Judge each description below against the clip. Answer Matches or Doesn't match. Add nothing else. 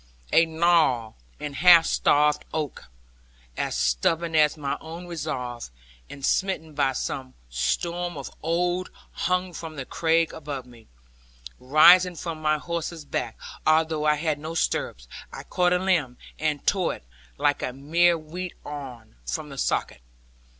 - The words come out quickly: Doesn't match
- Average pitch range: Matches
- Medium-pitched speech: Matches